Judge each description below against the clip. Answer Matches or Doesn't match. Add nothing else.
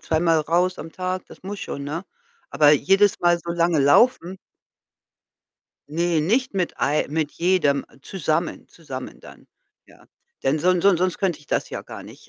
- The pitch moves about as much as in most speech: Matches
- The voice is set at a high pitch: Doesn't match